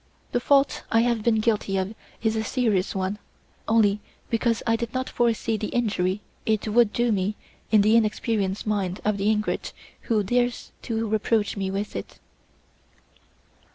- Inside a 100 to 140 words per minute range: No, average, 160 wpm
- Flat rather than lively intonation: Yes, narrow, 2.1 semitones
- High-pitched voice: Yes, high, 220 Hz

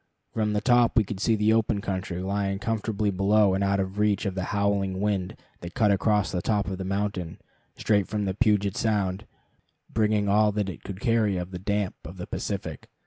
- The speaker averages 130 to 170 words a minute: No, average, 200 wpm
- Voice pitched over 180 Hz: No, low, 100 Hz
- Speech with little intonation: Yes, narrow, 1.9 semitones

